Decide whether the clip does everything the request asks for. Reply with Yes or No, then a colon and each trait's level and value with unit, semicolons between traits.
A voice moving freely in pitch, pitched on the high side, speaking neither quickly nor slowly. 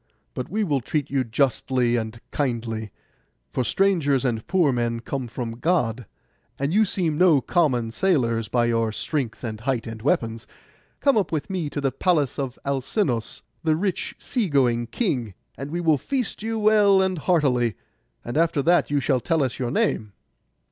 No: wide, 6.3 semitones; low, 135 Hz; average, 175 wpm